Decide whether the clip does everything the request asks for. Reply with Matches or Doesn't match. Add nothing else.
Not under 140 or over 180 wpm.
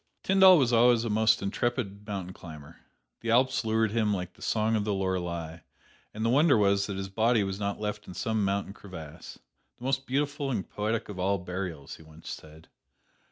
Doesn't match